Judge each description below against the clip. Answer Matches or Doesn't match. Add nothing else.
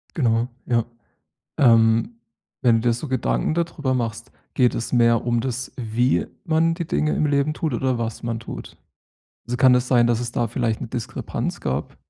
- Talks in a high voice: Doesn't match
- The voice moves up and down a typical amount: Doesn't match